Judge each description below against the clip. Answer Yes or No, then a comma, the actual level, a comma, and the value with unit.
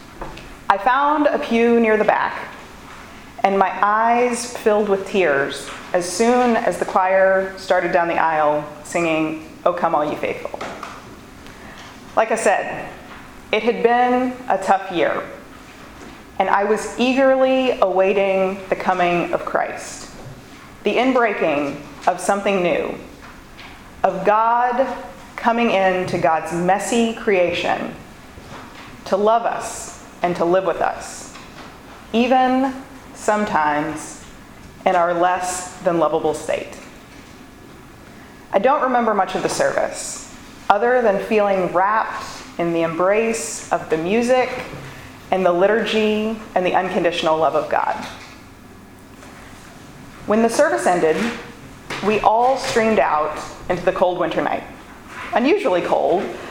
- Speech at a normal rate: No, slow, 120 wpm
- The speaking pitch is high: Yes, high, 195 Hz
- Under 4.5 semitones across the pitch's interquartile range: No, average, 4.8 semitones